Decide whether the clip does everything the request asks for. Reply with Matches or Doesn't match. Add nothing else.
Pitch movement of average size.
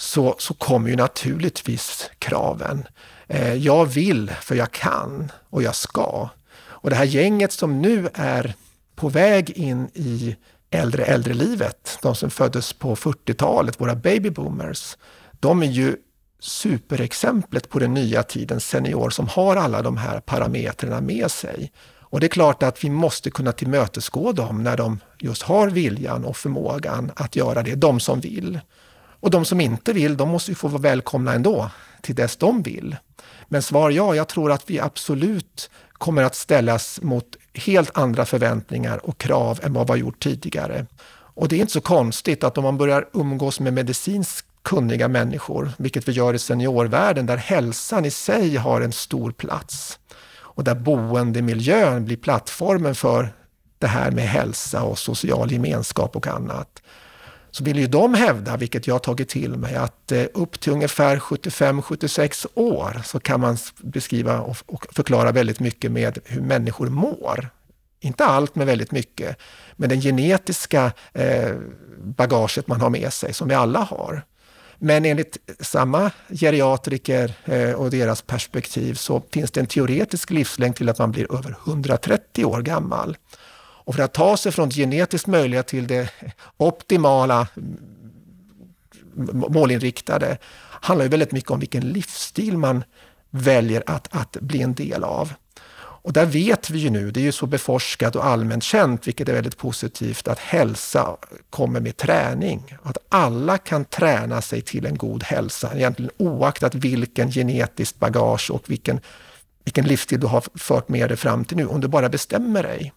Matches